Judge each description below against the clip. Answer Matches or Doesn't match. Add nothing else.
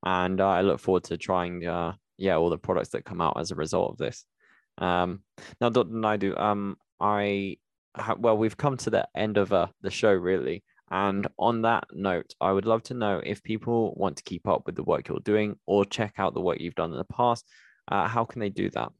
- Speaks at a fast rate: Matches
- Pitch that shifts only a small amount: Doesn't match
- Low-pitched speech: Matches